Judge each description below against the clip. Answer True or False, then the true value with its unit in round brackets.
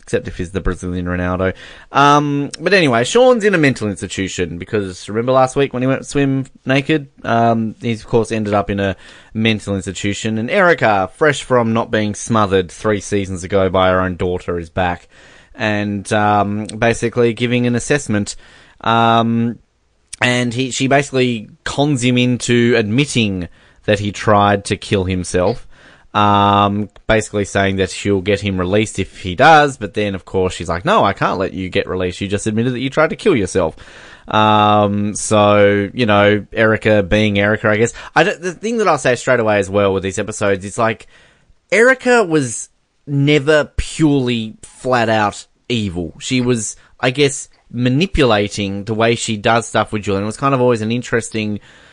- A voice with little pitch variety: False (3.8 semitones)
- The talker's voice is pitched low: True (110 Hz)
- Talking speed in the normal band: True (180 wpm)